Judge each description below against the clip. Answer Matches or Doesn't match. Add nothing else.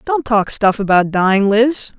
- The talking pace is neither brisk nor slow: Matches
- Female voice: Matches